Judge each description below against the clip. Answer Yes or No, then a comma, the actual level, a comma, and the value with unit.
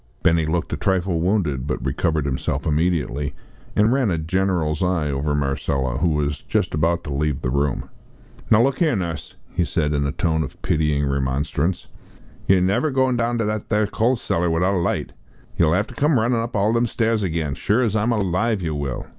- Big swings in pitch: Yes, wide, 6.3 semitones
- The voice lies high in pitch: No, very low, 85 Hz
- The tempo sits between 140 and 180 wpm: No, fast, 205 wpm